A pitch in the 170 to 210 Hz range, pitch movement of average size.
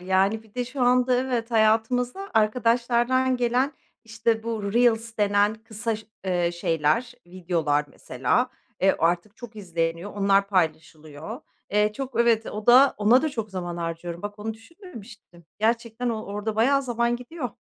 No: high, 220 Hz; average, 4.0 semitones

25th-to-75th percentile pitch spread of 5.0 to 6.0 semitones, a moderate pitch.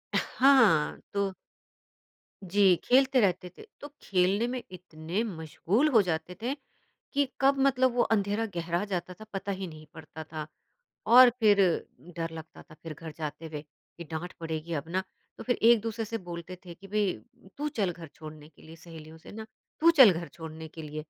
Yes: wide, 5.5 semitones; medium, 180 Hz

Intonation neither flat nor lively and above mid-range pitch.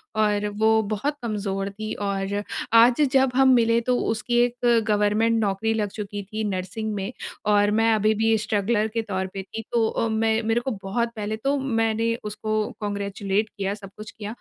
No: narrow, 1.9 semitones; high, 215 Hz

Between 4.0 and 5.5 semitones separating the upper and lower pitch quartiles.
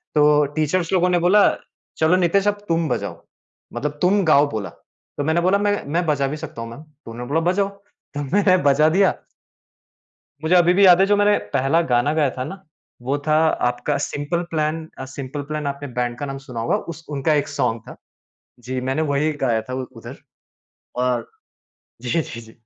Yes: average, 4.7 semitones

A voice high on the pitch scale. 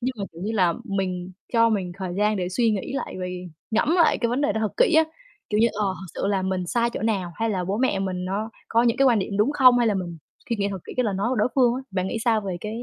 Yes: high, 210 Hz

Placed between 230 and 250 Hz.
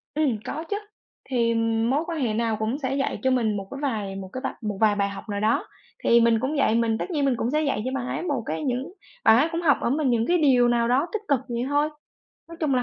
Yes: high, 245 Hz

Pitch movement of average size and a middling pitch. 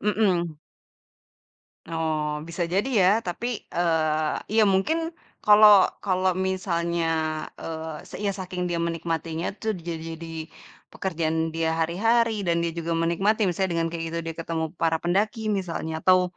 Yes: average, 3.0 semitones; medium, 170 Hz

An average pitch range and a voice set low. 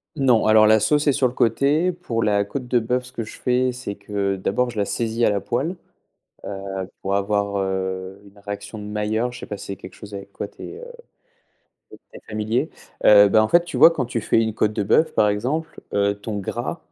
Yes: average, 3.7 semitones; low, 110 Hz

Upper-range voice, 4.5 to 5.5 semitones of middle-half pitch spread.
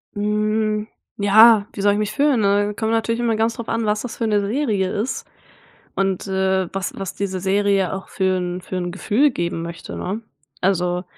No: high, 205 Hz; narrow, 2.6 semitones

